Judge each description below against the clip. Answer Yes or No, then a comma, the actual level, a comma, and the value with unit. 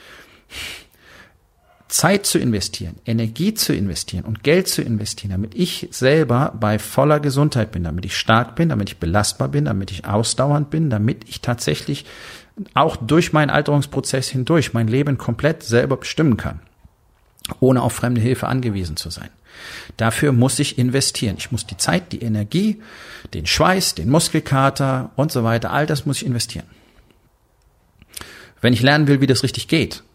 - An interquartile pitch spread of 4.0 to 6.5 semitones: Yes, wide, 5.4 semitones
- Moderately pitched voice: No, low, 120 Hz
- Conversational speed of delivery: Yes, average, 160 wpm